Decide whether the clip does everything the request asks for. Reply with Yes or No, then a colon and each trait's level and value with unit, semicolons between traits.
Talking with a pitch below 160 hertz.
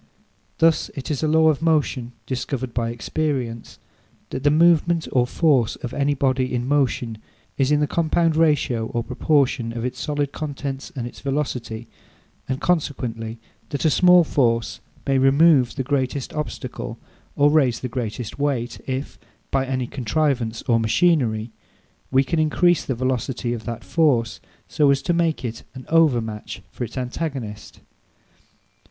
Yes: low, 135 Hz